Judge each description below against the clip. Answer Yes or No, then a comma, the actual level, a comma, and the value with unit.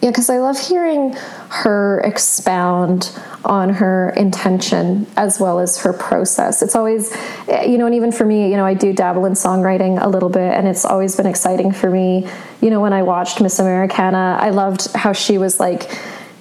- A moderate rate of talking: Yes, average, 195 wpm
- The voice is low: No, high, 195 Hz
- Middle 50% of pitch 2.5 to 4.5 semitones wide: Yes, average, 3.0 semitones